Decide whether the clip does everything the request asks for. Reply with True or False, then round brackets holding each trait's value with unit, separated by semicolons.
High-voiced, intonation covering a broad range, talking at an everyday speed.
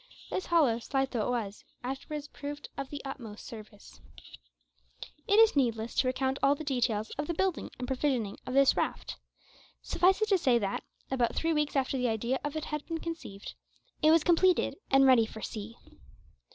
False (270 Hz; 4.5 semitones; 185 wpm)